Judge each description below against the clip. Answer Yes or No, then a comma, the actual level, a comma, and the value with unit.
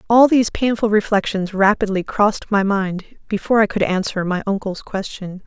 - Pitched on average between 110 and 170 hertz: No, high, 205 Hz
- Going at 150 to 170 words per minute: Yes, average, 165 wpm